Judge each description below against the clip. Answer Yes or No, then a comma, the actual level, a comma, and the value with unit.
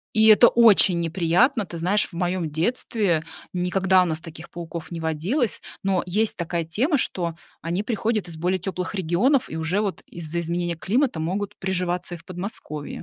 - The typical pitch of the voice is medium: Yes, medium, 180 Hz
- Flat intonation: No, average, 3.5 semitones